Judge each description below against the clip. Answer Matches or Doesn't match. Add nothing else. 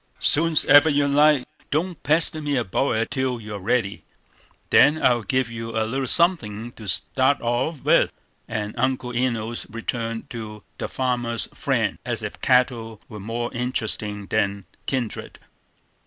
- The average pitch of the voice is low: Matches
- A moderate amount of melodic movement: Matches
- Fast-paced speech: Doesn't match